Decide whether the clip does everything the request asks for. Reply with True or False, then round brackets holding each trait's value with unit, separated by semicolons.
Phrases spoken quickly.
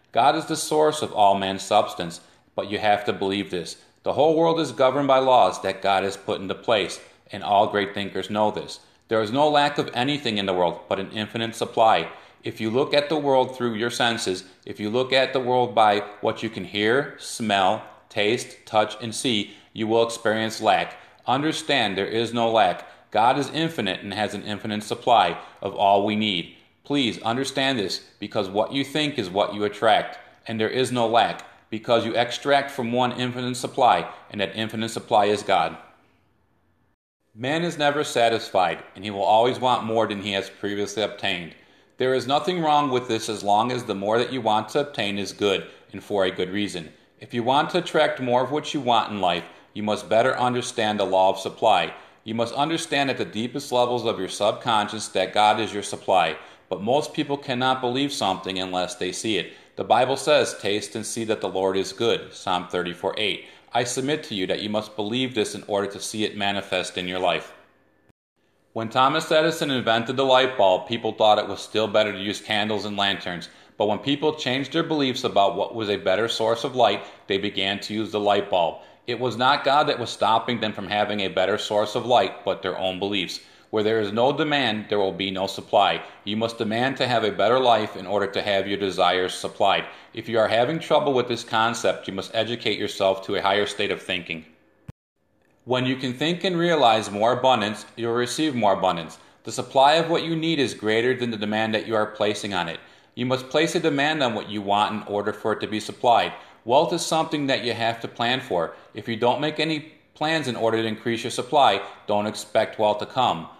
True (215 wpm)